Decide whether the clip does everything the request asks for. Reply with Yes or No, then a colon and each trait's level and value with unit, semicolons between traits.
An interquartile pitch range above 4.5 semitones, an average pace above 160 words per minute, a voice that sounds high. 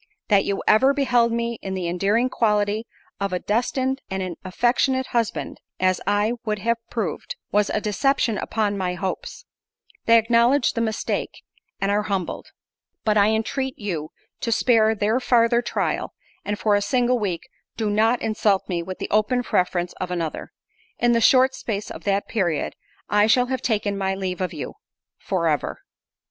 No: average, 3.5 semitones; average, 170 wpm; high, 210 Hz